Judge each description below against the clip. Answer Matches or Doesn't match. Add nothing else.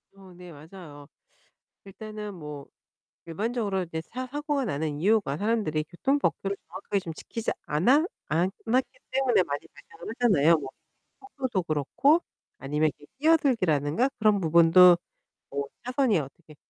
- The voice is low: Doesn't match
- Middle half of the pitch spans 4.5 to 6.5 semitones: Doesn't match